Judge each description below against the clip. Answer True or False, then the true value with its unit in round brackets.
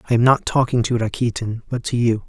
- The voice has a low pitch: True (120 Hz)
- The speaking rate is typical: False (235 wpm)